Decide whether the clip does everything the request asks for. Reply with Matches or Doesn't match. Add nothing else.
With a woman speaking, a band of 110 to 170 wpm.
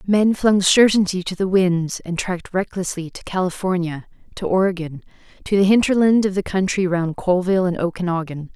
Matches